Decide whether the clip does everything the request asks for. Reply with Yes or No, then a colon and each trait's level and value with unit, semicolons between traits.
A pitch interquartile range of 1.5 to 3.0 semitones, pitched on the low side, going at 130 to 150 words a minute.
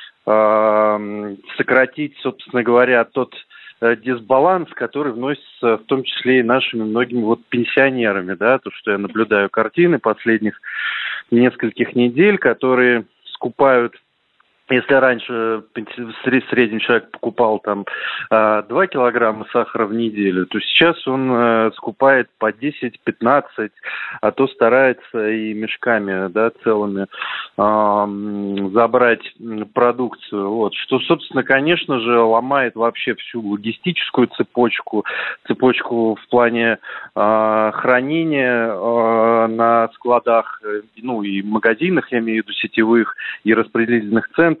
No: average, 2.7 semitones; low, 115 Hz; average, 115 wpm